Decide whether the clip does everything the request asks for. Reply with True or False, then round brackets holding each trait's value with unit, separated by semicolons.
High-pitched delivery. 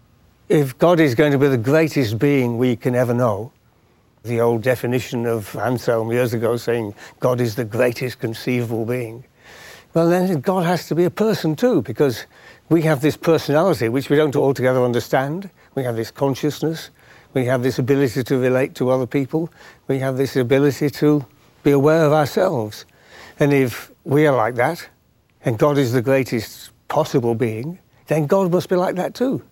False (135 Hz)